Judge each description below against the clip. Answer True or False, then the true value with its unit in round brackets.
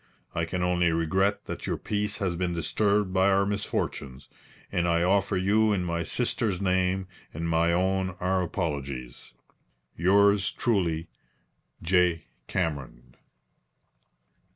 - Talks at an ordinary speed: False (125 wpm)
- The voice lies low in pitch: True (90 Hz)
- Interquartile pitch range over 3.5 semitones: False (2.9 semitones)